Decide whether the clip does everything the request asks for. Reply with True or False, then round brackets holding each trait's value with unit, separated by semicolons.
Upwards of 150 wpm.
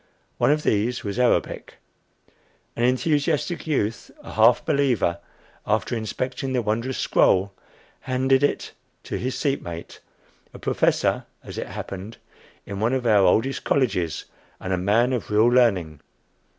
False (140 wpm)